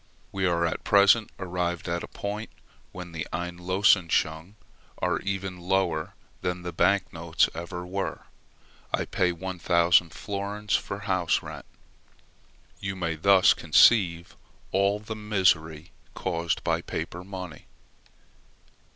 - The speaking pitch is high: No, very low, 90 Hz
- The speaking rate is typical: No, slow, 120 wpm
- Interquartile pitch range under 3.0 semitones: Yes, narrow, 2.4 semitones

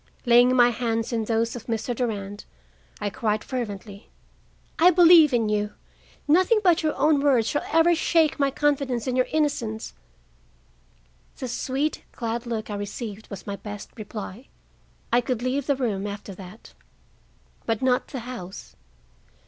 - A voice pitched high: Yes, high, 240 Hz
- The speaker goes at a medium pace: Yes, average, 150 wpm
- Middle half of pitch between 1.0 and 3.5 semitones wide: No, average, 4.5 semitones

